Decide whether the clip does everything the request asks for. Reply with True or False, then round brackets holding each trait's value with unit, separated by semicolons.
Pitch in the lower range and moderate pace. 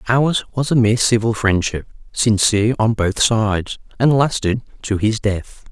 True (110 Hz; 160 wpm)